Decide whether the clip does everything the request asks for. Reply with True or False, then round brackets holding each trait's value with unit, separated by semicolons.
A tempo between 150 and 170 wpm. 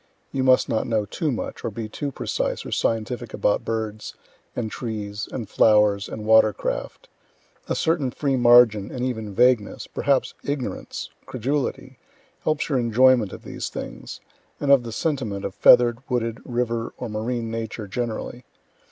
True (155 wpm)